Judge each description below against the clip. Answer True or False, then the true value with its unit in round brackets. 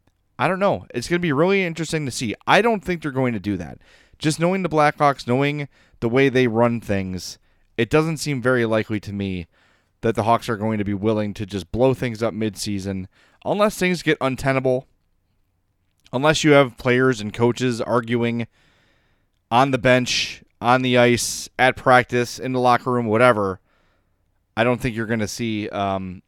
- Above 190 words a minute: False (185 wpm)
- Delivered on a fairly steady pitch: False (4.5 semitones)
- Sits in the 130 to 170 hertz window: False (120 Hz)